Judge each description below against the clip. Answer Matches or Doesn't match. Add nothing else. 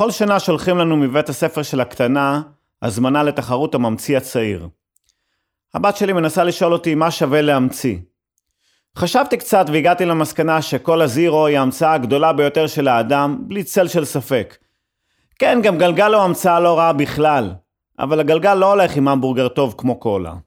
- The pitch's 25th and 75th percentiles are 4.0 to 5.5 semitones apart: Matches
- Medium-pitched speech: Matches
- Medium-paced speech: Doesn't match